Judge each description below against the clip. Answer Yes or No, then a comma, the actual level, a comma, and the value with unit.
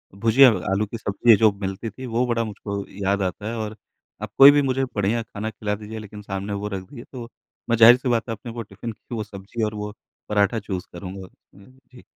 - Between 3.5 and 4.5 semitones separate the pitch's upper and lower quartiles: No, average, 2.7 semitones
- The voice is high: No, low, 110 Hz